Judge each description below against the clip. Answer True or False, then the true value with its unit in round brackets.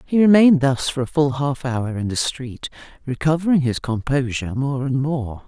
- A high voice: False (140 Hz)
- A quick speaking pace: False (185 wpm)